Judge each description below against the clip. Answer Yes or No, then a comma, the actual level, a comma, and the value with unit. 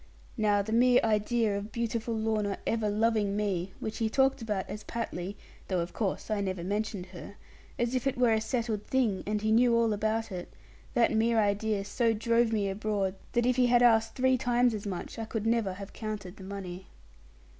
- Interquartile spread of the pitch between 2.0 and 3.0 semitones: Yes, narrow, 2.4 semitones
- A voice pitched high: Yes, high, 220 Hz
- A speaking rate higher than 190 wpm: Yes, average, 200 wpm